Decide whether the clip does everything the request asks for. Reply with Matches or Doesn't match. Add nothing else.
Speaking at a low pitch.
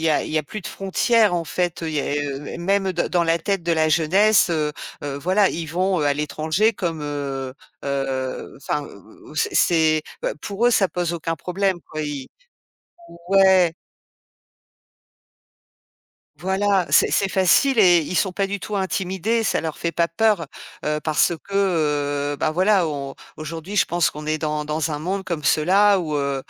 Doesn't match